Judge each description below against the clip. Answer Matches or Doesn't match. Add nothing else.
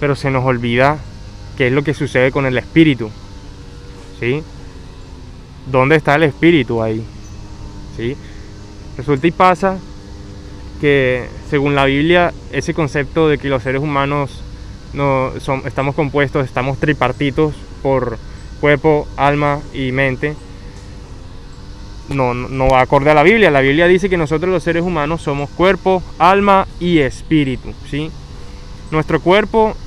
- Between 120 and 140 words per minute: Matches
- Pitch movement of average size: Doesn't match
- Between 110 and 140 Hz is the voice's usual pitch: Matches